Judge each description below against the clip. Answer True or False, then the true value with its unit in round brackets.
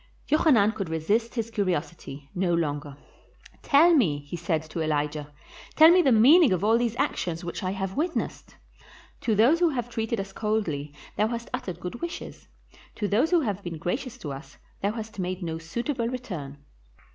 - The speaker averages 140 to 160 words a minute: False (180 wpm)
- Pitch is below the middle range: False (200 Hz)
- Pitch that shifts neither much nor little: False (6.4 semitones)